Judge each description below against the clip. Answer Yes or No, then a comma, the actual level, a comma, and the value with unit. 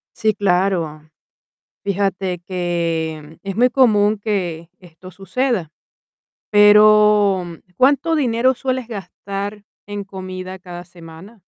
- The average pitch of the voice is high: Yes, high, 195 Hz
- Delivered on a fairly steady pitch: No, average, 3.3 semitones